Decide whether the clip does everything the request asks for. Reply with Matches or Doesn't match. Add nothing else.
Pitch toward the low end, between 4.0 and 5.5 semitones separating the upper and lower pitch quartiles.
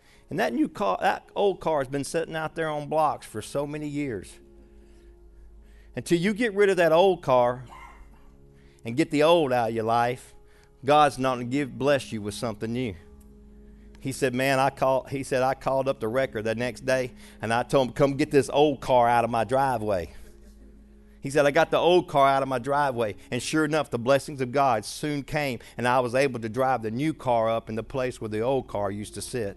Matches